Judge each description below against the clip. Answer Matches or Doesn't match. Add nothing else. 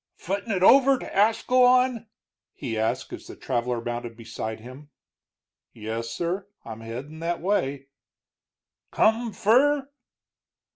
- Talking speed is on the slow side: Matches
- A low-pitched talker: Doesn't match